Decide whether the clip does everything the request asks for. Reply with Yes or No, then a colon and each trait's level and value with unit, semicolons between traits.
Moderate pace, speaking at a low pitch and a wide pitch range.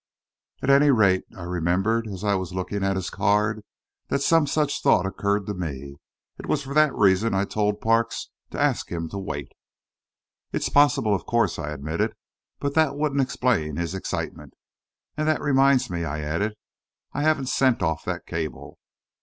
Yes: average, 175 wpm; low, 105 Hz; wide, 7.4 semitones